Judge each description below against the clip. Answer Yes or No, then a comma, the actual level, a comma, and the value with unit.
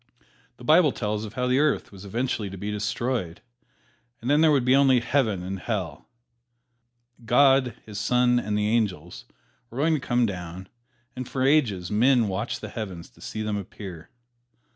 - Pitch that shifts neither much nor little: Yes, average, 4.6 semitones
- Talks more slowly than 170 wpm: No, average, 175 wpm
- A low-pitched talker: Yes, low, 110 Hz